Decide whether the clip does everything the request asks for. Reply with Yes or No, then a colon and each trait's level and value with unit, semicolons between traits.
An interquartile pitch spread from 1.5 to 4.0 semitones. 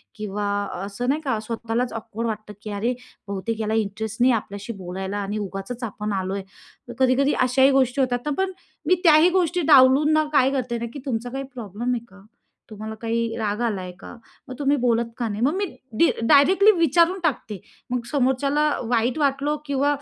No: average, 4.6 semitones